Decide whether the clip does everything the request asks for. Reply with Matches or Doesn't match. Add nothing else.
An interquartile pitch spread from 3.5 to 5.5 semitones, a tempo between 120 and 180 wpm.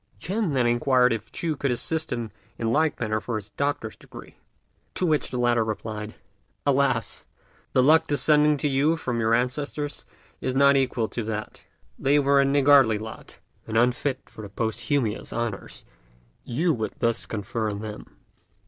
Matches